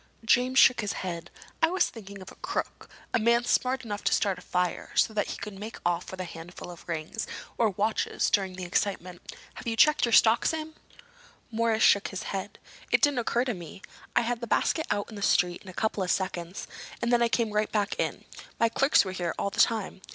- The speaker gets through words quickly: Yes, fast, 225 wpm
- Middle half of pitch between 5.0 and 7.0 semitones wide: No, average, 4.2 semitones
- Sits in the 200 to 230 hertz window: Yes, high, 210 Hz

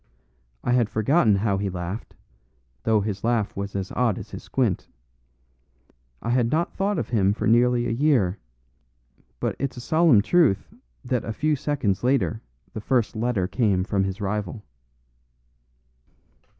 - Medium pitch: No, low, 115 Hz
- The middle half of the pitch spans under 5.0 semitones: Yes, average, 4.0 semitones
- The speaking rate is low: No, average, 150 wpm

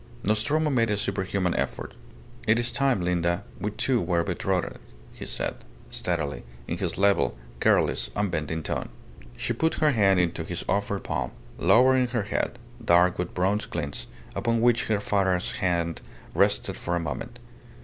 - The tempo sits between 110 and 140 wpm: No, average, 155 wpm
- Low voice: Yes, low, 100 Hz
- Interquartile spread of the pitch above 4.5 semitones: Yes, average, 5.0 semitones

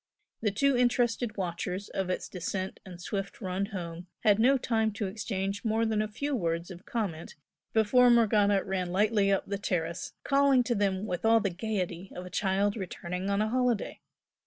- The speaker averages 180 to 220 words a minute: Yes, average, 185 wpm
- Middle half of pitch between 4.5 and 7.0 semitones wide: No, average, 3.3 semitones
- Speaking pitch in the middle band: No, high, 200 Hz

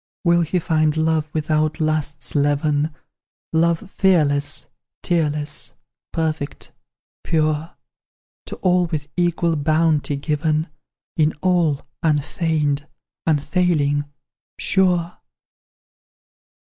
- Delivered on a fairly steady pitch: Yes, narrow, 2.1 semitones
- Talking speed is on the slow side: Yes, slow, 85 wpm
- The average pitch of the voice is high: No, medium, 155 Hz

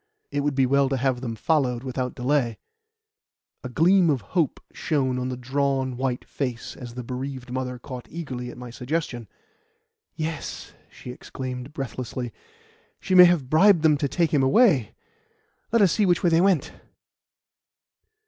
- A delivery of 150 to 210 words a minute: Yes, average, 160 wpm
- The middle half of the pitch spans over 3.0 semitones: Yes, average, 3.8 semitones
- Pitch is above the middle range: No, low, 135 Hz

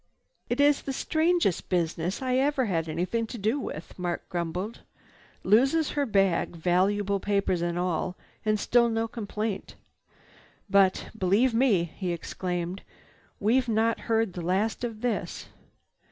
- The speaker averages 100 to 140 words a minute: Yes, slow, 135 wpm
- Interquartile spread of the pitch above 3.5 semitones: Yes, average, 4.8 semitones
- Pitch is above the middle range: Yes, high, 205 Hz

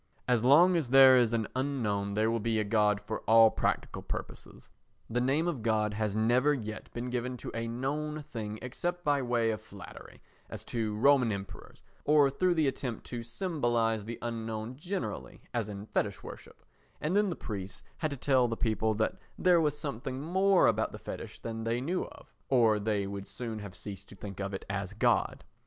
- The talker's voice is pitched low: Yes, low, 115 Hz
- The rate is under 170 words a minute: No, average, 195 wpm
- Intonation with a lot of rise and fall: No, average, 4.4 semitones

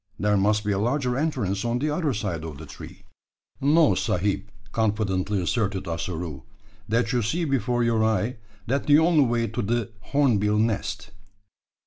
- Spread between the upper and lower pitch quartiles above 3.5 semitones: Yes, average, 3.9 semitones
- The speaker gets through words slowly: No, average, 160 wpm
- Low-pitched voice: Yes, low, 110 Hz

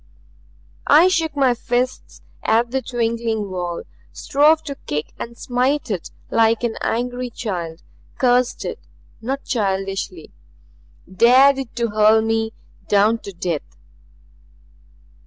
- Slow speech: Yes, slow, 120 wpm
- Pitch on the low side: No, high, 235 Hz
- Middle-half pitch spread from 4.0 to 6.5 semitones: No, average, 3.5 semitones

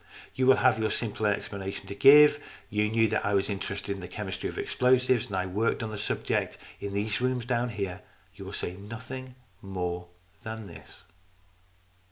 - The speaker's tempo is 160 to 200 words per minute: Yes, average, 190 wpm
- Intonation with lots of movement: No, average, 3.9 semitones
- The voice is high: No, low, 105 Hz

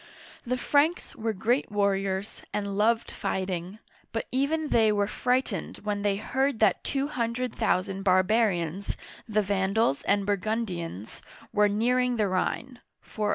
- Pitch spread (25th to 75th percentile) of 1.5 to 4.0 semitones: Yes, average, 3.4 semitones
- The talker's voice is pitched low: No, high, 210 Hz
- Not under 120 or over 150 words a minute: Yes, average, 140 wpm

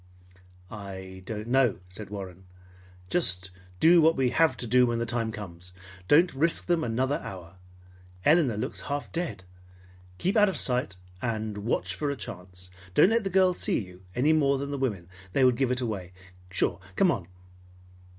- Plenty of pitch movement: Yes, wide, 7.3 semitones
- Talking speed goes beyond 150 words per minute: Yes, average, 175 wpm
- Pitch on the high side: No, low, 120 Hz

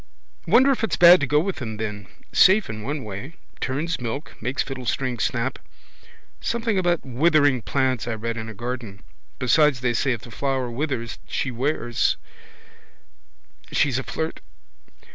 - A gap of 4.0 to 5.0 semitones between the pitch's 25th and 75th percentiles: Yes, average, 4.6 semitones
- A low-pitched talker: Yes, low, 130 Hz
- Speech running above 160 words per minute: No, average, 155 wpm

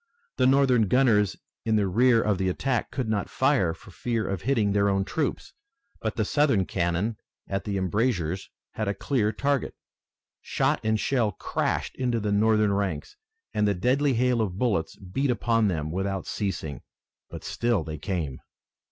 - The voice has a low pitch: Yes, low, 105 Hz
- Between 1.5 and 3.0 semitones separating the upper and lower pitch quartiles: No, average, 4.2 semitones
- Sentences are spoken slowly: No, average, 170 wpm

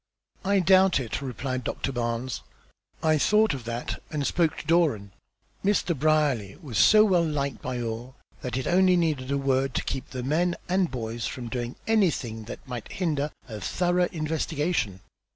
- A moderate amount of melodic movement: No, wide, 5.9 semitones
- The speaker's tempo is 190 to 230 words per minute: No, average, 170 wpm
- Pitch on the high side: No, medium, 140 Hz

